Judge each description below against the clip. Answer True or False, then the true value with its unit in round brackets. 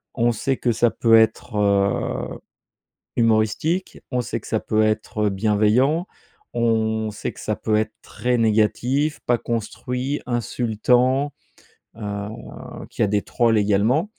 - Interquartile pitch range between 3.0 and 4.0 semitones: False (2.6 semitones)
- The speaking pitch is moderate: False (115 Hz)